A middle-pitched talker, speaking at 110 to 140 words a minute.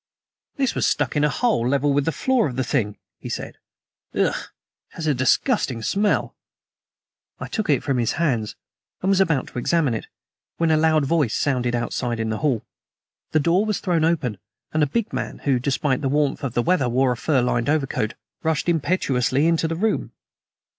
No: medium, 145 Hz; average, 195 wpm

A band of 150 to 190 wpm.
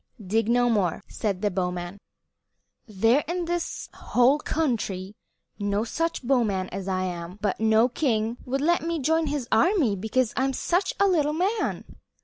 Yes: average, 165 wpm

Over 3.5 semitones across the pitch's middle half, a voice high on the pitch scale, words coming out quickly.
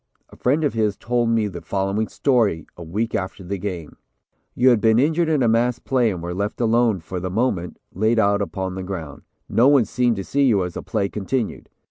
No: average, 4.3 semitones; low, 110 Hz; fast, 220 wpm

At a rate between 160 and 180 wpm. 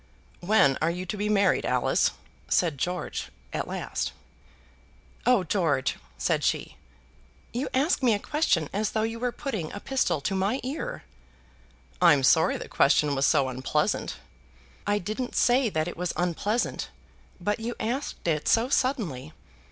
No: average, 150 wpm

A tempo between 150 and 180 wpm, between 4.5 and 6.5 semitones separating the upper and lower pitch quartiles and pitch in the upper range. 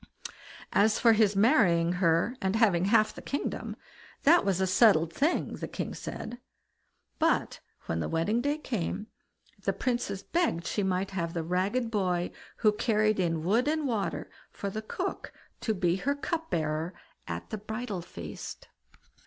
Yes: average, 160 wpm; average, 5.0 semitones; high, 200 Hz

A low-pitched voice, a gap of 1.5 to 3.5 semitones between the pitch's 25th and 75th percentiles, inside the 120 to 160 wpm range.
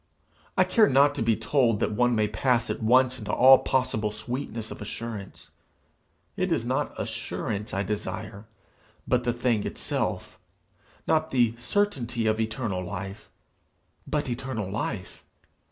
Yes: low, 115 Hz; average, 3.2 semitones; average, 140 wpm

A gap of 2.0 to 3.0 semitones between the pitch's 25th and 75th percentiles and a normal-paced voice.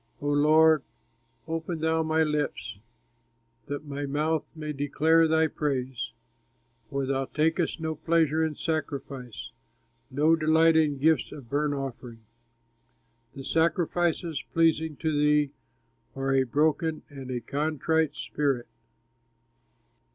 No: average, 2.7 semitones; slow, 115 wpm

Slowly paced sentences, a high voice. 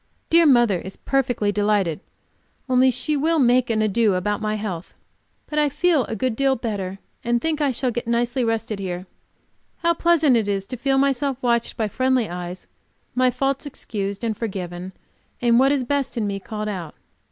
No: average, 185 wpm; high, 235 Hz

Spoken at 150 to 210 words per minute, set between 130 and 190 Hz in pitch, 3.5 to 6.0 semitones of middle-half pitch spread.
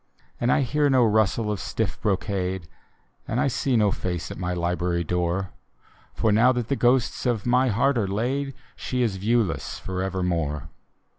No: average, 165 wpm; low, 105 Hz; average, 5.1 semitones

